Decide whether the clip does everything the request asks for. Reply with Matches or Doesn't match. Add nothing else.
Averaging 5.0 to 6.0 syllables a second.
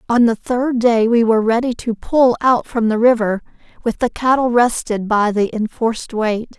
Doesn't match